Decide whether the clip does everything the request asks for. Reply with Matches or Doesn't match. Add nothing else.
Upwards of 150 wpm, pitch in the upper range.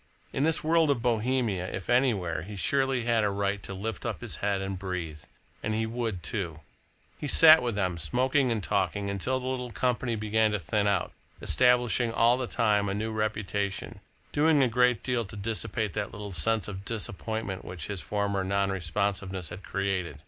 Doesn't match